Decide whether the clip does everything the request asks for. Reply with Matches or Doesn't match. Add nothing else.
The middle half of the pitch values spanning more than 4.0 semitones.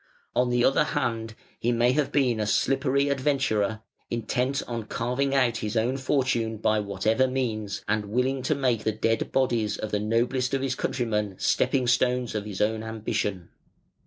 Doesn't match